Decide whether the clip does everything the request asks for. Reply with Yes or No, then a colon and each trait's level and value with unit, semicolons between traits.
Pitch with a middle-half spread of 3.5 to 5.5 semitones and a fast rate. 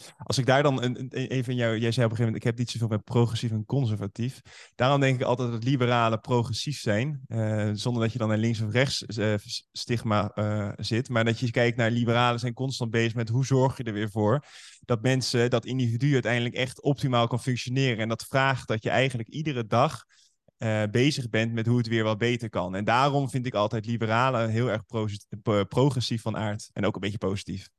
No: narrow, 2.6 semitones; fast, 220 wpm